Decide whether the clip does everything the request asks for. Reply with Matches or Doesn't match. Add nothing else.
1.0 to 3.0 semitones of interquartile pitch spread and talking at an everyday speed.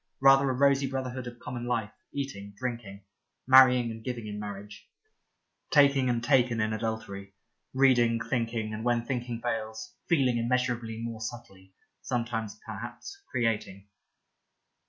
Doesn't match